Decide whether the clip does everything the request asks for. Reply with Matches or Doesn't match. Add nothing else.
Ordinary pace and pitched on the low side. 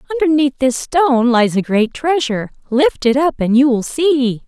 Doesn't match